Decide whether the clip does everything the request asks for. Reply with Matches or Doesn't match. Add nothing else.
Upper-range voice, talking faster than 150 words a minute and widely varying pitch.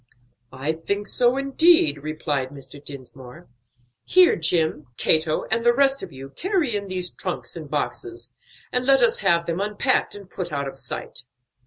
Doesn't match